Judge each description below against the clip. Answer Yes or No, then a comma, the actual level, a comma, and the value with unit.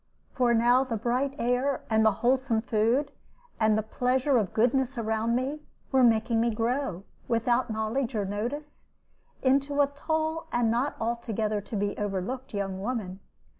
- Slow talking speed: No, average, 155 wpm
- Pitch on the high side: Yes, high, 235 Hz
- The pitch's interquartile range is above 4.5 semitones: No, average, 3.2 semitones